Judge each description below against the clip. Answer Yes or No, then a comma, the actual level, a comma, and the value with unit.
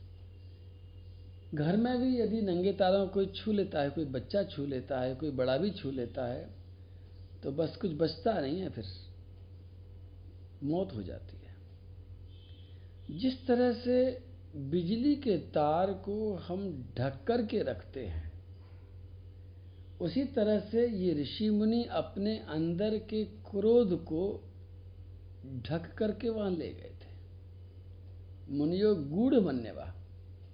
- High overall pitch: No, low, 130 Hz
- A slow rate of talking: No, average, 130 wpm